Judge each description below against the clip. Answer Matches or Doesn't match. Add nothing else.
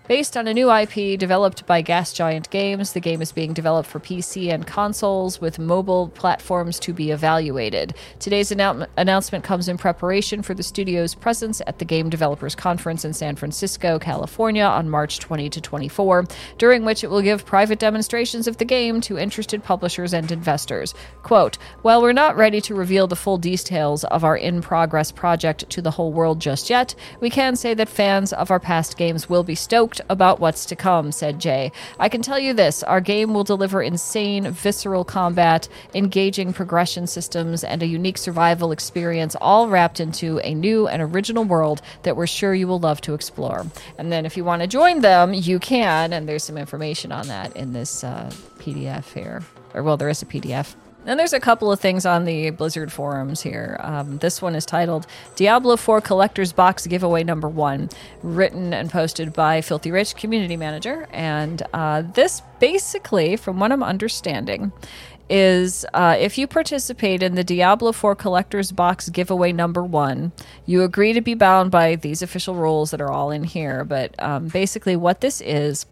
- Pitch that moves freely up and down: Doesn't match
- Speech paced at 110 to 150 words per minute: Doesn't match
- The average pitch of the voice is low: Doesn't match